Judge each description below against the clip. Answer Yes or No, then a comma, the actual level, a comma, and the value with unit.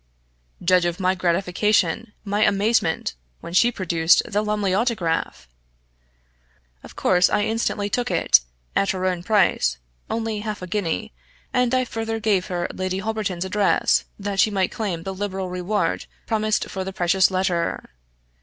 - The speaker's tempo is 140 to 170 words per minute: Yes, average, 150 wpm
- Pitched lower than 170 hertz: No, high, 195 Hz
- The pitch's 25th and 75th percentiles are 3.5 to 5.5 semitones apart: No, average, 2.9 semitones